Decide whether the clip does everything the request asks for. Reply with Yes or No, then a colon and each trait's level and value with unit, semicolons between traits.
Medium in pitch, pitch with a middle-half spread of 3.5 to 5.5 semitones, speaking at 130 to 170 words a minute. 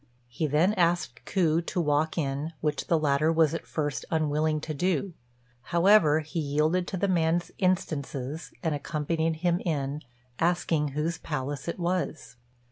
No: medium, 160 Hz; narrow, 2.5 semitones; average, 150 wpm